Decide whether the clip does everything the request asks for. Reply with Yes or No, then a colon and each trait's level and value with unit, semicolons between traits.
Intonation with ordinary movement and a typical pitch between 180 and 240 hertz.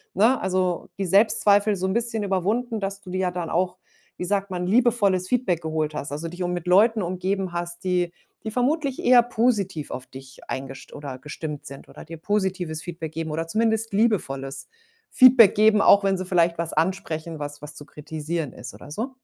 Yes: average, 4.7 semitones; medium, 185 Hz